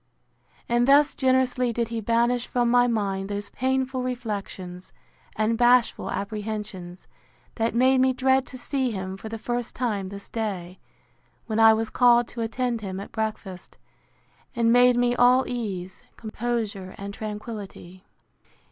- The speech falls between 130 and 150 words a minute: Yes, average, 145 wpm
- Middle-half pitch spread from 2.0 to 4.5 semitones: Yes, average, 3.3 semitones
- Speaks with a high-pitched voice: Yes, high, 230 Hz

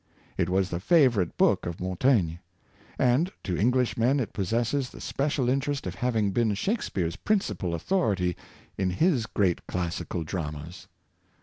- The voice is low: Yes, low, 105 Hz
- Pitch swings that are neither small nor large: No, wide, 6.6 semitones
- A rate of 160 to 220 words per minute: No, average, 140 wpm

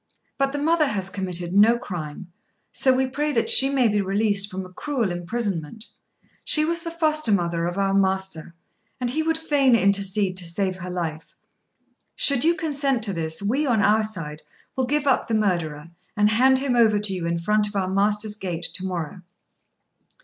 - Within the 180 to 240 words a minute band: Yes, average, 190 wpm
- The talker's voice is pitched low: No, high, 205 Hz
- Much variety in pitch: Yes, wide, 6.2 semitones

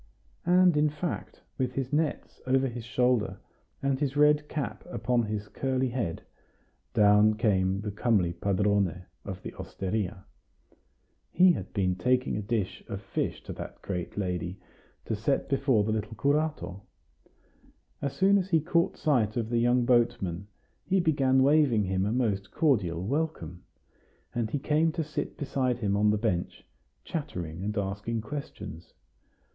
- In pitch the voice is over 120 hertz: No, low, 115 Hz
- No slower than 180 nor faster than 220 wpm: No, average, 150 wpm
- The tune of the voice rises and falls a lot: Yes, wide, 6.0 semitones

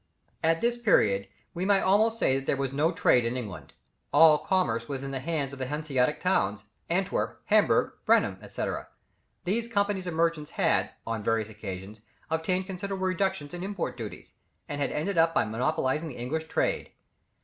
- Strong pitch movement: Yes, wide, 6.6 semitones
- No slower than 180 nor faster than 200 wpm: No, average, 170 wpm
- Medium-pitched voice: Yes, medium, 155 Hz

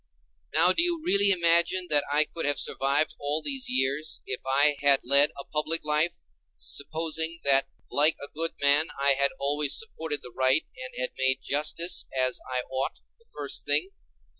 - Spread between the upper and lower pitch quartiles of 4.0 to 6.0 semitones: No, average, 3.3 semitones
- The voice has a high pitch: No, medium, 150 Hz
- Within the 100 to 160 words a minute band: No, average, 175 wpm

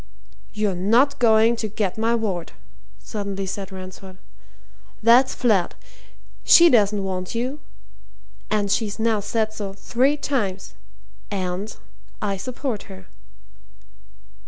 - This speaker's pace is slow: Yes, slow, 110 wpm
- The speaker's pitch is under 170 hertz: No, high, 210 Hz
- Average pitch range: Yes, average, 3.2 semitones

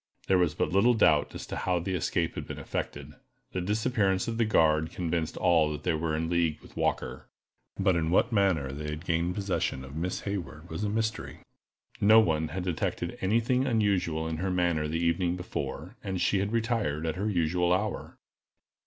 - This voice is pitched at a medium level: No, very low, 90 Hz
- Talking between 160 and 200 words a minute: Yes, average, 195 wpm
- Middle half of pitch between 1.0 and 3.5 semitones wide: No, average, 4.0 semitones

